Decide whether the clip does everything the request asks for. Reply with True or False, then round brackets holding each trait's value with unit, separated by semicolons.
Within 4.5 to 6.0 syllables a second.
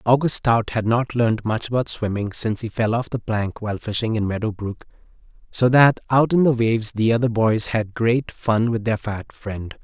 True (5.0 syllables/s)